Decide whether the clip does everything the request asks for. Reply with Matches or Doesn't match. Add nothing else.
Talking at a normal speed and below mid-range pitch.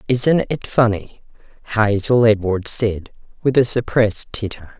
Doesn't match